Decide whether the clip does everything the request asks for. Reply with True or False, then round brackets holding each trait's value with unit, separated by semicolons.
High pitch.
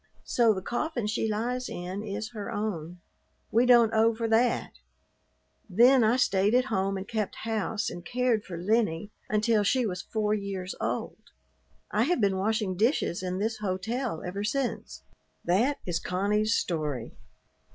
True (215 Hz)